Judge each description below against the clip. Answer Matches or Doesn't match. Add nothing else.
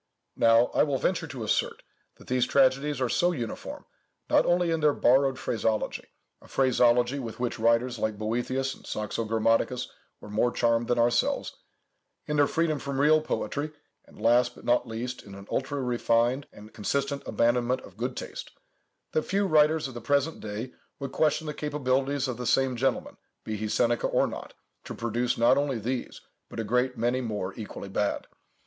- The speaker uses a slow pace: Doesn't match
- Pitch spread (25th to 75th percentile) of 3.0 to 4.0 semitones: Matches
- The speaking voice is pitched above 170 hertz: Doesn't match